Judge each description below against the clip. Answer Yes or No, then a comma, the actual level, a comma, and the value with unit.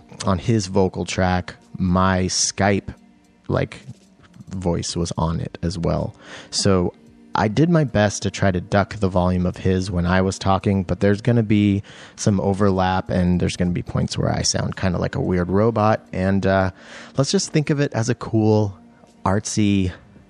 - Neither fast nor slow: Yes, average, 185 wpm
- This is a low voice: Yes, very low, 95 Hz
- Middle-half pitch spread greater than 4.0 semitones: No, average, 2.7 semitones